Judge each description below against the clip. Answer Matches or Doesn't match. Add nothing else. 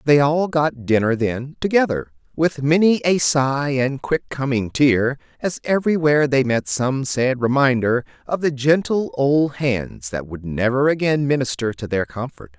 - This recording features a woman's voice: Doesn't match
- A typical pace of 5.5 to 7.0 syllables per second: Doesn't match